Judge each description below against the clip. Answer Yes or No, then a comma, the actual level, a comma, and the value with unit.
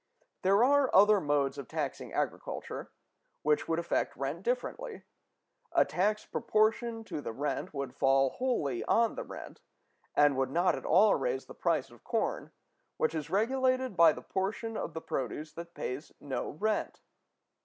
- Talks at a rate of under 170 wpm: Yes, average, 160 wpm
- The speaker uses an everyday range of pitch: No, wide, 7.5 semitones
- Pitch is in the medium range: Yes, medium, 170 Hz